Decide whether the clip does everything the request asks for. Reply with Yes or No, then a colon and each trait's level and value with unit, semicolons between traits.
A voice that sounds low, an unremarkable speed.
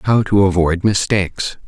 Yes: very low, 95 Hz; average, 145 wpm